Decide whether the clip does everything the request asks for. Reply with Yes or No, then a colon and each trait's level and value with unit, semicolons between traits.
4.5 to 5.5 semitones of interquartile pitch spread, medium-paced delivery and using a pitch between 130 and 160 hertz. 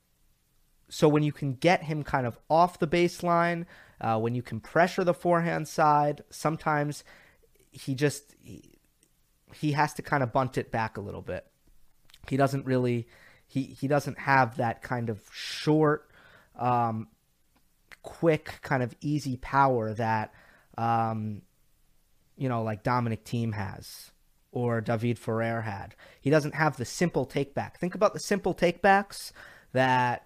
Yes: average, 5.1 semitones; average, 150 wpm; low, 135 Hz